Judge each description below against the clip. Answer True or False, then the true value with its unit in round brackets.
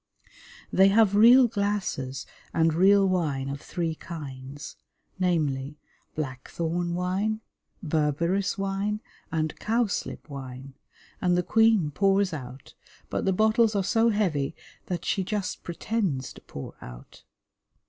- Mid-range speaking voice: True (180 Hz)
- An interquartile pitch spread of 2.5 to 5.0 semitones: False (5.6 semitones)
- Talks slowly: True (120 wpm)